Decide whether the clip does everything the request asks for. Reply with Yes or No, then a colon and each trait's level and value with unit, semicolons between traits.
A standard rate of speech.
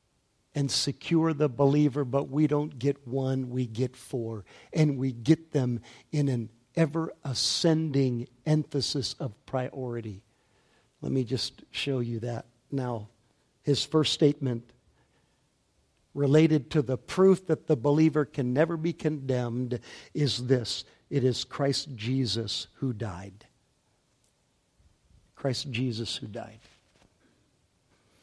No: slow, 115 wpm